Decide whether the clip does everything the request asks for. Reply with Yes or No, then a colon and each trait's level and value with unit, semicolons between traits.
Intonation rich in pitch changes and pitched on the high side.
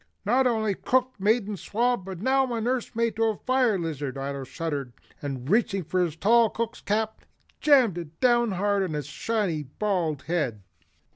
Yes: wide, 6.4 semitones; high, 200 Hz